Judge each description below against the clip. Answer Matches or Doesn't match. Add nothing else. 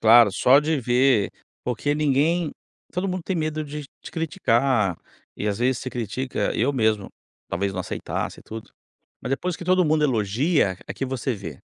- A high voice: Doesn't match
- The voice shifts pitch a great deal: Matches